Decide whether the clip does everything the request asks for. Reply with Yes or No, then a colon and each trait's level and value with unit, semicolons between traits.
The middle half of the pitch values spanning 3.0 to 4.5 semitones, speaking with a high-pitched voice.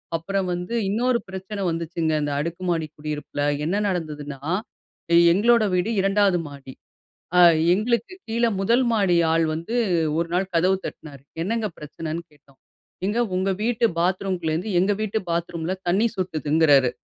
No: average, 4.1 semitones; medium, 180 Hz